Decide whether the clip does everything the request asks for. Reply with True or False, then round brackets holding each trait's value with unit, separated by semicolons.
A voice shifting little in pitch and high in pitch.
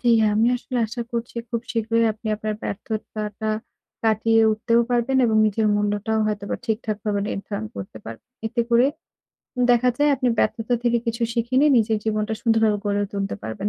True (1.9 semitones; 220 Hz)